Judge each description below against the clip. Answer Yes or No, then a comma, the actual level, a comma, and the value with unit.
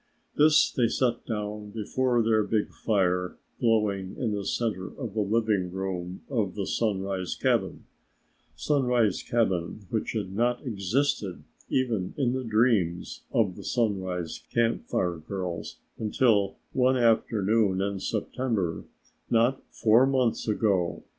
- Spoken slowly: Yes, slow, 125 wpm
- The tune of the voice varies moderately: Yes, average, 3.8 semitones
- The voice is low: Yes, low, 105 Hz